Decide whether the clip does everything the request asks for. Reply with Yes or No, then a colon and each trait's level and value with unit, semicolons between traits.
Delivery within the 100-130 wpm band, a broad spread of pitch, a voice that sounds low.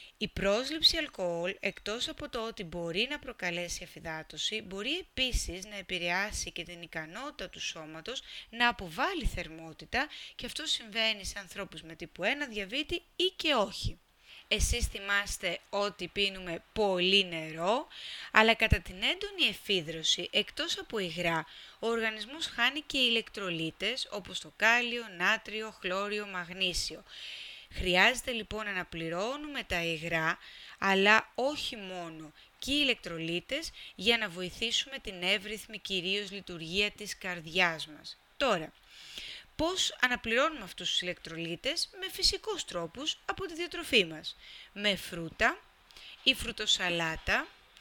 No: average, 125 wpm; wide, 6.0 semitones; high, 205 Hz